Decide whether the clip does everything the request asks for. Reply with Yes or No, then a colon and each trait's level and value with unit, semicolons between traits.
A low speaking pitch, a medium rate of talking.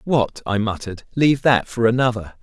Yes: low, 115 Hz; average, 175 wpm